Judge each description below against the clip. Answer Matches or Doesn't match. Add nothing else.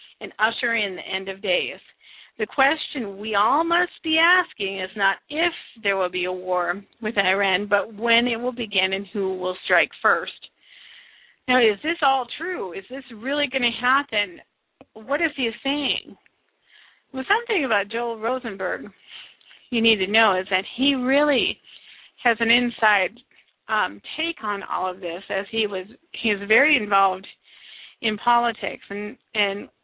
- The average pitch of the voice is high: Matches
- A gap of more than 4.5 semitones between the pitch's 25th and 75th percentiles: Matches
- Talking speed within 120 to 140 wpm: Doesn't match